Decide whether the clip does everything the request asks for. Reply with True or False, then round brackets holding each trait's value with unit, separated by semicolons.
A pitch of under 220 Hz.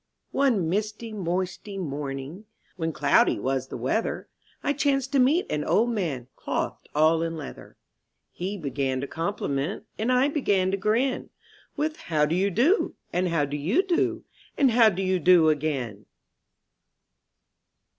True (185 Hz)